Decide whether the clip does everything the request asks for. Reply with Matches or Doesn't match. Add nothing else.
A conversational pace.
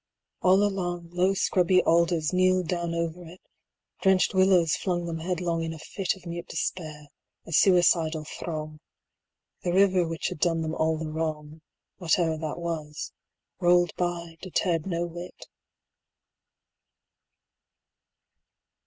Doesn't match